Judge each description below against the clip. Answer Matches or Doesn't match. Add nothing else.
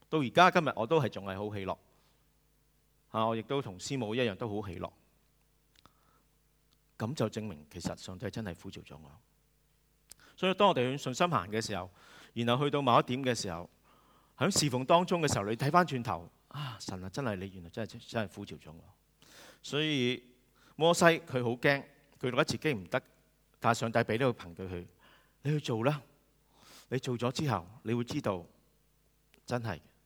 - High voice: Doesn't match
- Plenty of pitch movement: Matches